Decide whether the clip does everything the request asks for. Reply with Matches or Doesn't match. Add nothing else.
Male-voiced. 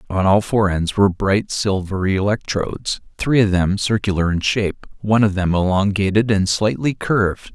Matches